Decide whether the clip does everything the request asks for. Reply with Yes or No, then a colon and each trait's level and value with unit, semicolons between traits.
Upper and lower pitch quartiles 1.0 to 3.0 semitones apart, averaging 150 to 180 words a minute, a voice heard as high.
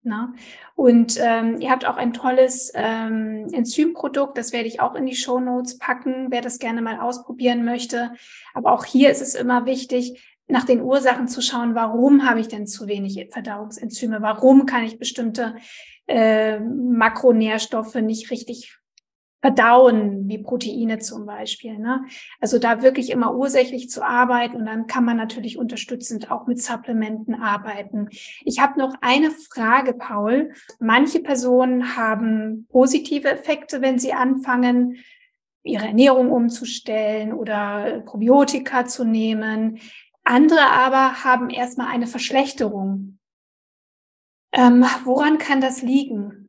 No: narrow, 2.6 semitones; average, 135 wpm; high, 245 Hz